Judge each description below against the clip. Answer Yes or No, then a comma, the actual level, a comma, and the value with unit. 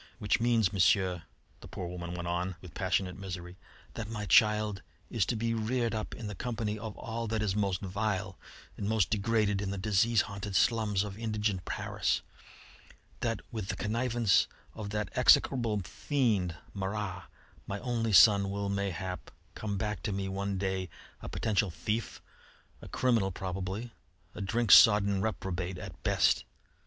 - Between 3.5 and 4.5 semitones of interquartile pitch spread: No, average, 2.7 semitones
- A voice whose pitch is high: No, low, 100 Hz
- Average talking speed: Yes, average, 160 wpm